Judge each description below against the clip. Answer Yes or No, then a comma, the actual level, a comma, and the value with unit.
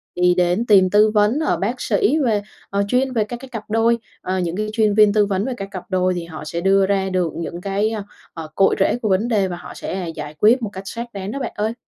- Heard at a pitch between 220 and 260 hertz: No, high, 200 Hz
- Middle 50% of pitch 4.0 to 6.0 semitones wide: No, average, 3.2 semitones